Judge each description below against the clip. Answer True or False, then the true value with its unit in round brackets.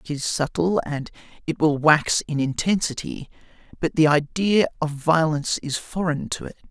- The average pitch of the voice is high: False (155 Hz)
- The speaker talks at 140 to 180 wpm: True (160 wpm)